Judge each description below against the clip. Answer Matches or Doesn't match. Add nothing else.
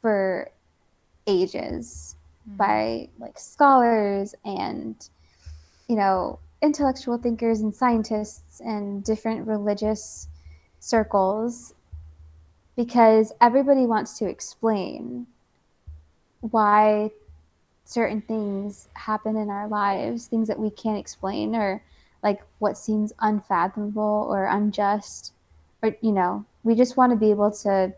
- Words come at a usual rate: Doesn't match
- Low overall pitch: Doesn't match